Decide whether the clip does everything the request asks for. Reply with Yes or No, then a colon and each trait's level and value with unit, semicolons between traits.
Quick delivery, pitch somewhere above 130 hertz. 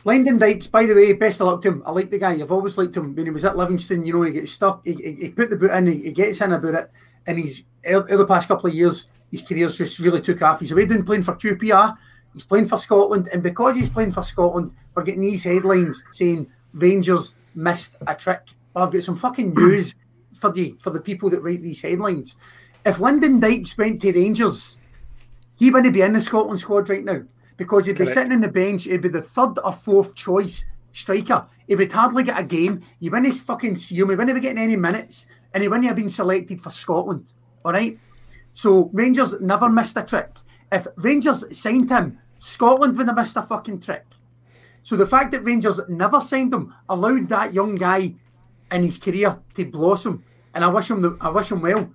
Yes: fast, 225 wpm; high, 190 Hz